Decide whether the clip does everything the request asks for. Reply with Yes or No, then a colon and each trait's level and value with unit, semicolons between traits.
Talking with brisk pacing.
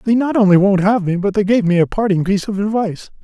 Yes: fast, 280 wpm